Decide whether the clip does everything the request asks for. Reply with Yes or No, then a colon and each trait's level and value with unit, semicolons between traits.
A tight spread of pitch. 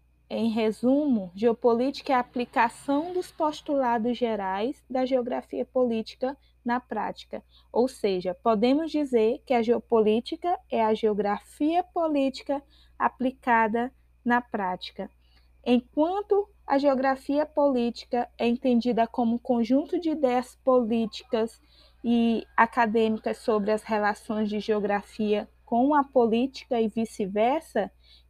No: average, 3.2 semitones